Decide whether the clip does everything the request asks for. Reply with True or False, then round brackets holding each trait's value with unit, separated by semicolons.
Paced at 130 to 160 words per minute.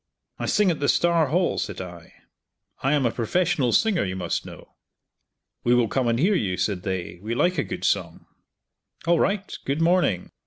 False (190 wpm)